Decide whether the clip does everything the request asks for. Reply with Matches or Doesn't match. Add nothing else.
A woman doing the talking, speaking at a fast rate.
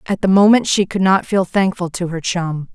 Matches